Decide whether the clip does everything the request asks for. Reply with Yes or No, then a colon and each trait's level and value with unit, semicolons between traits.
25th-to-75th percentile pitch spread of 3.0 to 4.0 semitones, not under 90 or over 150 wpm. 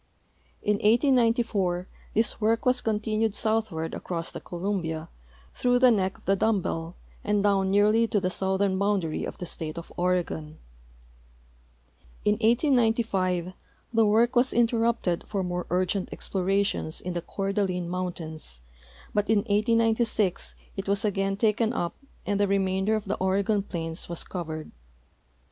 Yes: average, 3.5 semitones; average, 145 wpm